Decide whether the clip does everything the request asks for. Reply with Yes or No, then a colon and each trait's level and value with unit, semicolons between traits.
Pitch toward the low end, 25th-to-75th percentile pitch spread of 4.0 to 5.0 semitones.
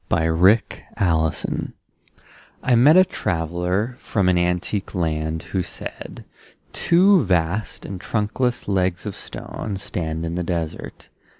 Yes: very low, 90 Hz; average, 4.3 semitones